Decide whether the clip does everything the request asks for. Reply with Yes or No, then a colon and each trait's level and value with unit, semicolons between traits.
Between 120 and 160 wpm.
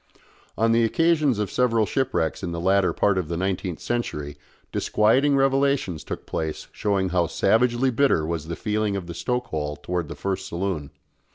No: average, 175 wpm